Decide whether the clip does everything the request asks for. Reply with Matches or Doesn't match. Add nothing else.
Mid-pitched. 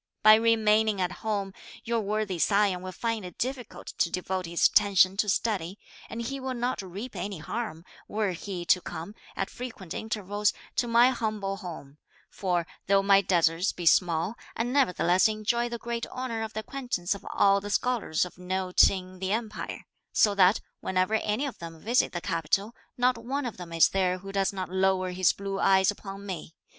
Doesn't match